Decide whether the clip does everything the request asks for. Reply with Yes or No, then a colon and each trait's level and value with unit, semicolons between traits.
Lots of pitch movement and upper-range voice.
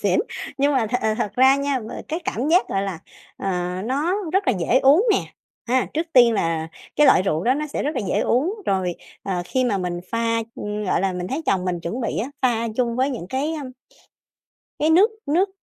Yes: wide, 6.7 semitones; high, 245 Hz